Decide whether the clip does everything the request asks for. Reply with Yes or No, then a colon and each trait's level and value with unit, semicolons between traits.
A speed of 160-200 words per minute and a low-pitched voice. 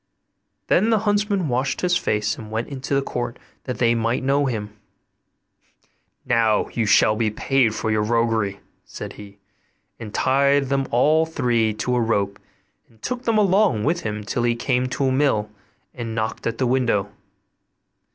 Yes: average, 170 wpm; low, 120 Hz